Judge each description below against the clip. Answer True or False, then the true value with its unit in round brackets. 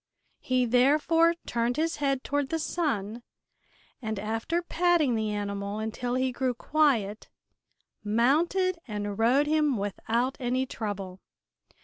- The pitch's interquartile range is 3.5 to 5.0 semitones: False (5.6 semitones)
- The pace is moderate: False (120 wpm)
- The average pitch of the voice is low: False (250 Hz)